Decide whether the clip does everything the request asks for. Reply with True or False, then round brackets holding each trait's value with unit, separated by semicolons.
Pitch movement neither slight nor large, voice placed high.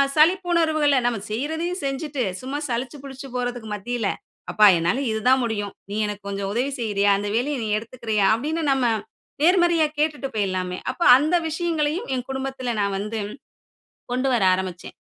False (5.9 semitones; 255 Hz)